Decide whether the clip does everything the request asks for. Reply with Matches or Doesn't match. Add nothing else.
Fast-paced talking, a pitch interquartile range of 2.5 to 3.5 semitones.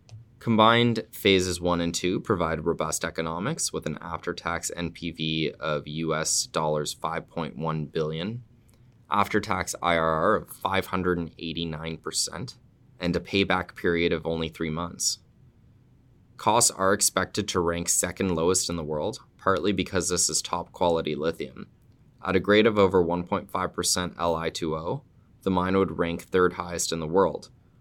Doesn't match